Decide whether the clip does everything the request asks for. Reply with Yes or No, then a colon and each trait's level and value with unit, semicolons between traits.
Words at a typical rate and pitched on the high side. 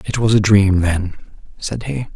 No: average, 195 wpm; low, 100 Hz